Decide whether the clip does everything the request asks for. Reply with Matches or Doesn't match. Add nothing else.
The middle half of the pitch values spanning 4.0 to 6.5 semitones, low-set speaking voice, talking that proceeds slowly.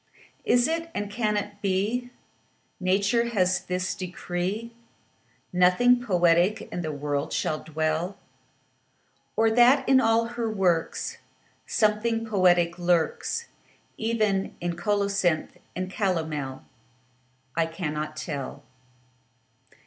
Doesn't match